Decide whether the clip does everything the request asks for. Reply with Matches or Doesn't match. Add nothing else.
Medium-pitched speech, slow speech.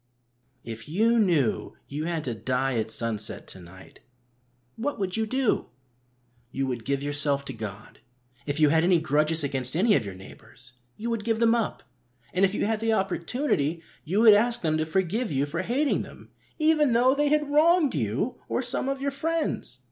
Doesn't match